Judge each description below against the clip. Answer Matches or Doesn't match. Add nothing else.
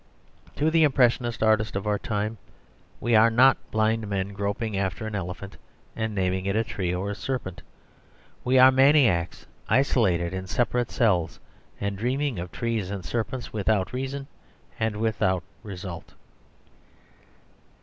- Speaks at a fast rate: Doesn't match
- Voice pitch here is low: Matches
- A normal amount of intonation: Matches